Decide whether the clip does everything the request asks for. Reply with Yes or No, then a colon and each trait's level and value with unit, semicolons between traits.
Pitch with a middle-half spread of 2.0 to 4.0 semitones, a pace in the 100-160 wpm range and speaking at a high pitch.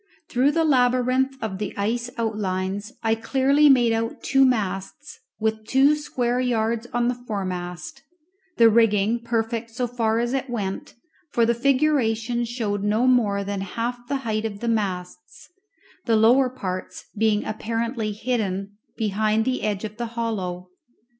Yes: average, 2.9 semitones; average, 150 wpm; high, 230 Hz